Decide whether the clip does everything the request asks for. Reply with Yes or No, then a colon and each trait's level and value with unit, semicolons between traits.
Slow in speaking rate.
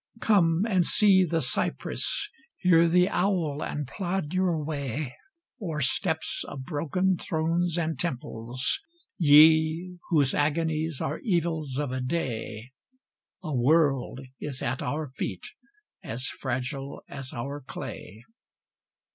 Yes: slow, 120 wpm